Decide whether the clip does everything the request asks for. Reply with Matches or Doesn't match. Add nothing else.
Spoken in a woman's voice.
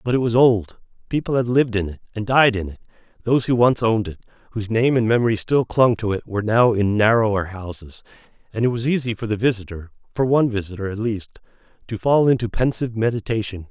Doesn't match